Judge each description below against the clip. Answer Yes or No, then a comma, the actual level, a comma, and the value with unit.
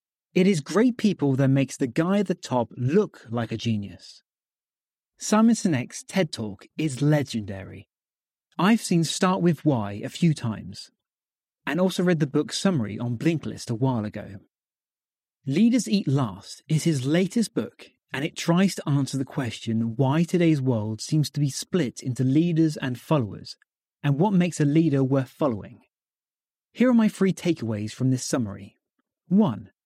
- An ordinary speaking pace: Yes, average, 165 wpm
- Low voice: No, medium, 150 Hz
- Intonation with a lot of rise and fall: Yes, wide, 7.0 semitones